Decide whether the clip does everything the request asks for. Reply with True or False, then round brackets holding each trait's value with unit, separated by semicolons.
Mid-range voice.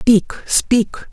False (225 Hz)